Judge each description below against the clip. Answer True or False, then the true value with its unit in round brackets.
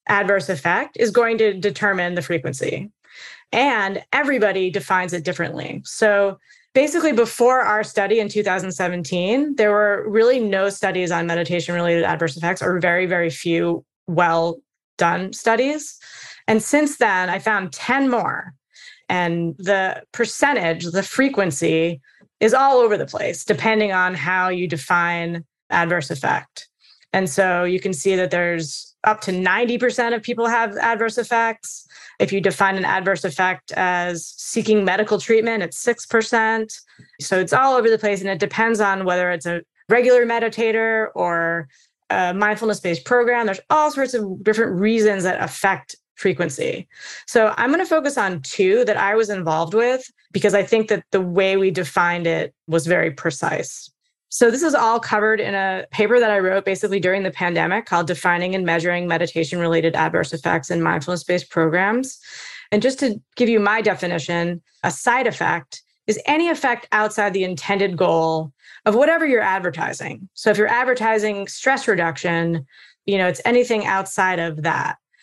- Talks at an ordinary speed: True (160 wpm)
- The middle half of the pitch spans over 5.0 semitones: False (4.5 semitones)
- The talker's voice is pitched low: False (195 Hz)